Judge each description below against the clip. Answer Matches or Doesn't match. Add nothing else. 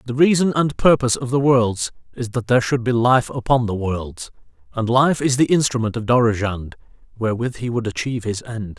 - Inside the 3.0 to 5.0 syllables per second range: Doesn't match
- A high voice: Doesn't match